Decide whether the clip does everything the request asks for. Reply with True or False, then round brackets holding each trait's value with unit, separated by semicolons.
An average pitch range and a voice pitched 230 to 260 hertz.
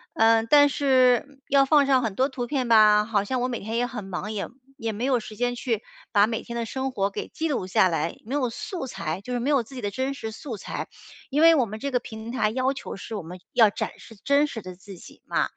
True (3.9 semitones; 235 Hz)